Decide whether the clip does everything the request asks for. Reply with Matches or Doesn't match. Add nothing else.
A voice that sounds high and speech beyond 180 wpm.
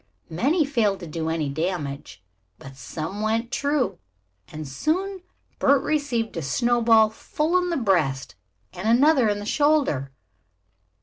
Doesn't match